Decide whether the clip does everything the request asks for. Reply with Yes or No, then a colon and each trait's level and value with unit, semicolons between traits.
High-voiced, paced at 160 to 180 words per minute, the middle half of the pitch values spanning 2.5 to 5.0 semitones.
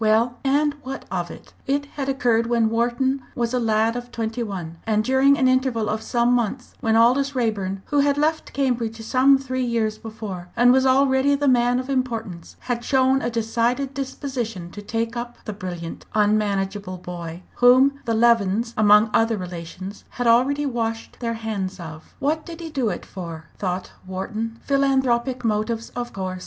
Yes: high, 235 Hz; average, 175 wpm; average, 3.6 semitones